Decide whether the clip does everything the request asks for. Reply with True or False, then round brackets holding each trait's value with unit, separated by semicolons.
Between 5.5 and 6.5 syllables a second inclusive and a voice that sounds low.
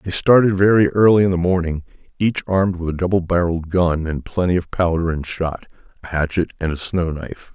True (5.9 syllables/s; 90 Hz)